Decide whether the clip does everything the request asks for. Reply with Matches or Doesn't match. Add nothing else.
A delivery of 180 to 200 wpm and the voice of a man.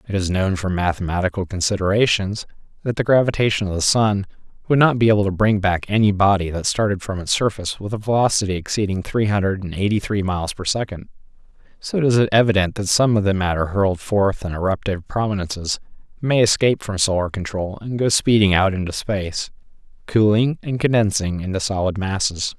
Matches